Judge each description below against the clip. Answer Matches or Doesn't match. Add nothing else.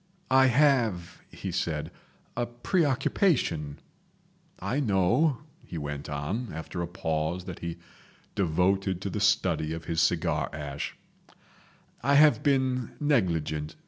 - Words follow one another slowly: Matches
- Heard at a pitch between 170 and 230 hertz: Doesn't match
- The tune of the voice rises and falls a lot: Matches